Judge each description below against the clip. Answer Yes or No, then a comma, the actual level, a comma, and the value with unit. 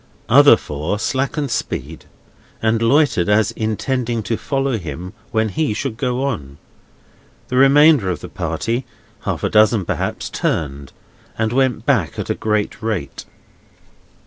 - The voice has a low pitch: Yes, low, 110 Hz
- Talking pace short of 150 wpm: Yes, average, 140 wpm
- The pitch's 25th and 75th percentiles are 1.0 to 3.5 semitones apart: No, average, 4.5 semitones